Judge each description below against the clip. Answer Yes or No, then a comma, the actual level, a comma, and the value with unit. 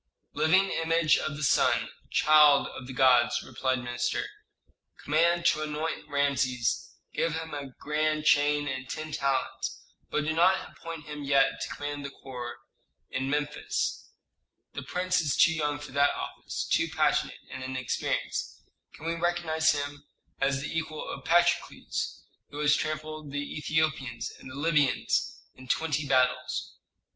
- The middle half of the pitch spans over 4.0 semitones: No, narrow, 2.6 semitones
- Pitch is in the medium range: Yes, medium, 150 Hz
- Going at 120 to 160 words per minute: Yes, average, 150 wpm